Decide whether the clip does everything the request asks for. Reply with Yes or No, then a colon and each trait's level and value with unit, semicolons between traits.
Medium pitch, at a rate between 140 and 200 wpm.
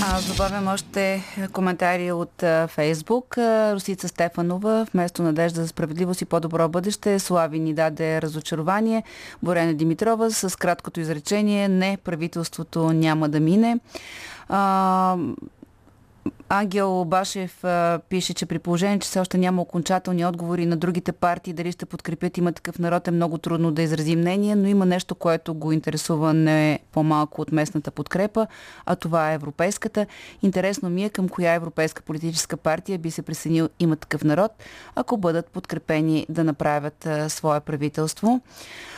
Yes: medium, 175 Hz; average, 145 wpm